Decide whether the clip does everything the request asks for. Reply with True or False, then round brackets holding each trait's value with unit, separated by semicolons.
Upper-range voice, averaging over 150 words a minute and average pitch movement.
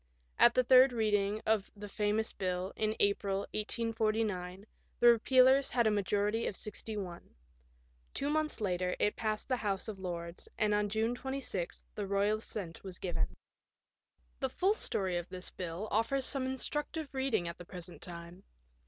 True (210 Hz; 160 wpm; 4.1 semitones)